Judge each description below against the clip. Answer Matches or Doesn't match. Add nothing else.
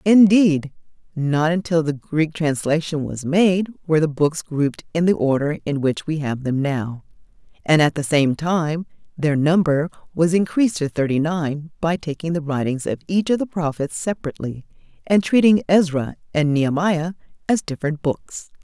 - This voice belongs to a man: Doesn't match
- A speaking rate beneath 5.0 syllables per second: Matches